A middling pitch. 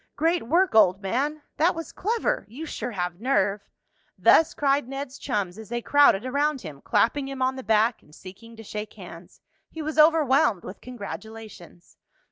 No: high, 245 Hz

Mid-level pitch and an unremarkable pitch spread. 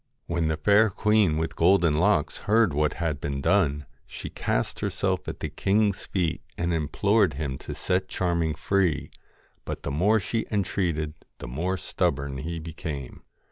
No: very low, 85 Hz; average, 4.5 semitones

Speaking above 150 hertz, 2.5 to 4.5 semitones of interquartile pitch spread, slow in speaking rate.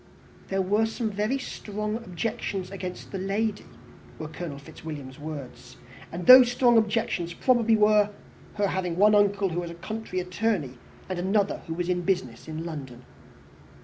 No: high, 190 Hz; average, 4.2 semitones; average, 155 wpm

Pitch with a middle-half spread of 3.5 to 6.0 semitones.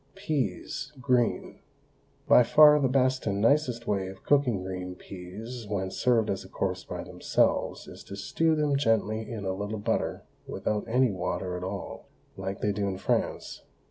Yes: average, 5.1 semitones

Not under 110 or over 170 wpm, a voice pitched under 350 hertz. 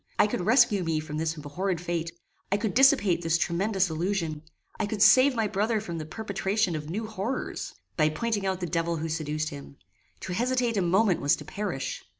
No: average, 195 wpm; medium, 185 Hz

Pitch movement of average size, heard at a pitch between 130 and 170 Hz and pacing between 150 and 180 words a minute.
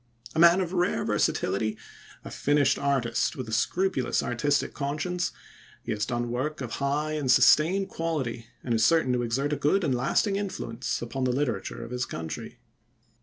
Yes: average, 4.8 semitones; medium, 140 Hz; average, 170 wpm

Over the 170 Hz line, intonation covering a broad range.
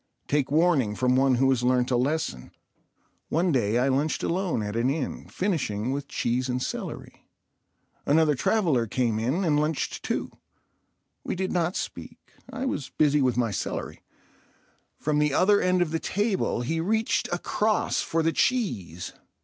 No: medium, 145 Hz; wide, 5.8 semitones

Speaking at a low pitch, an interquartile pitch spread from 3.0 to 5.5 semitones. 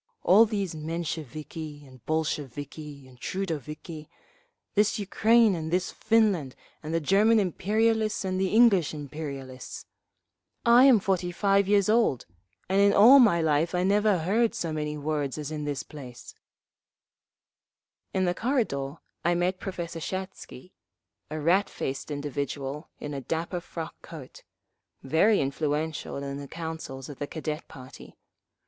No: medium, 165 Hz; average, 5.0 semitones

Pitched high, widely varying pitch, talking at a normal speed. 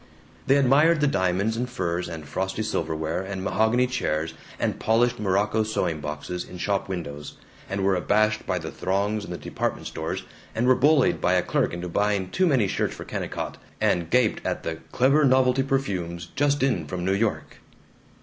No: low, 100 Hz; wide, 6.0 semitones; average, 180 wpm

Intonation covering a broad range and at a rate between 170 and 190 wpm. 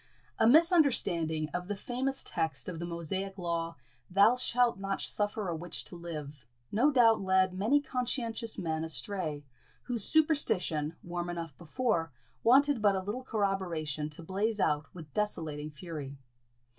No: wide, 5.7 semitones; average, 145 wpm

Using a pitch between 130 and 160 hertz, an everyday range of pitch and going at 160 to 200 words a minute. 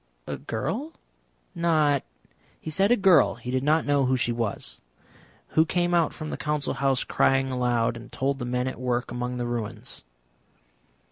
Yes: low, 135 Hz; average, 4.2 semitones; average, 180 wpm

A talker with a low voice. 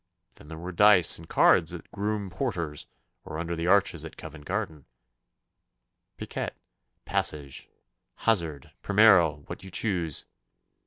Yes: very low, 85 Hz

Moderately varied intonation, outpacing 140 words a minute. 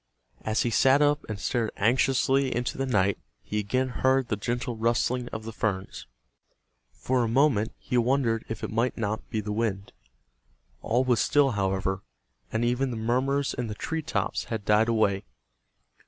Yes: average, 3.3 semitones; average, 170 wpm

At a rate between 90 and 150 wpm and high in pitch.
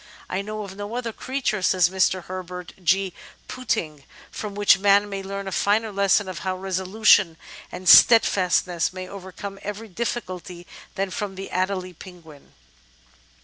Yes: average, 145 wpm; high, 195 Hz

